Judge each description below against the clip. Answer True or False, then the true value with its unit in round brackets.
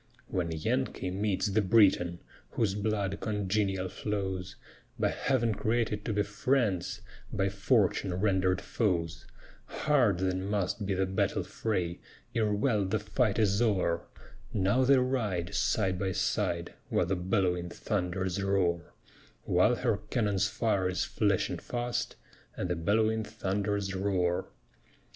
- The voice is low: True (100 Hz)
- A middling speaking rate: False (130 wpm)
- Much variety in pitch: False (2.7 semitones)